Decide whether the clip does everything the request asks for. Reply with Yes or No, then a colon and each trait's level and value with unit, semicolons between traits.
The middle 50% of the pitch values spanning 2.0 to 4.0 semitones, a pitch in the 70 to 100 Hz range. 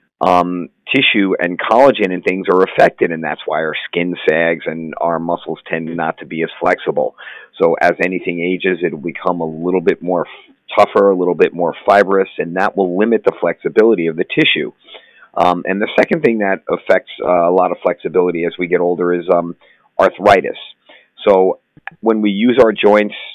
Yes: average, 2.7 semitones; very low, 90 Hz